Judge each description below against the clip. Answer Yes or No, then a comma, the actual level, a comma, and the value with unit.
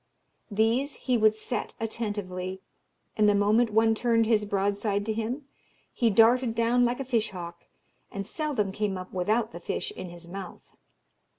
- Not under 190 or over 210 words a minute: No, average, 165 wpm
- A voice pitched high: Yes, high, 215 Hz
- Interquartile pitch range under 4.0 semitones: Yes, average, 2.9 semitones